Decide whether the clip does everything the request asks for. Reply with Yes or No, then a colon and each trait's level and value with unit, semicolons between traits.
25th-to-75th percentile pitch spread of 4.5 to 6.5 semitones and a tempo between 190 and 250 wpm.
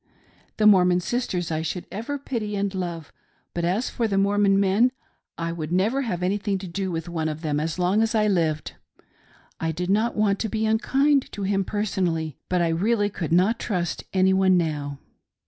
No: average, 3.8 semitones; average, 195 wpm